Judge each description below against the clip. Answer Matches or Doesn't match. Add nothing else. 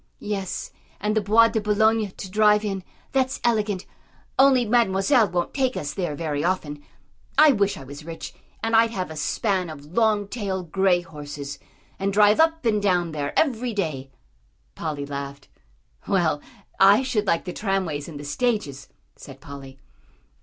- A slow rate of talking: Doesn't match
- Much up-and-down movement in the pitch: Matches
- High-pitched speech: Matches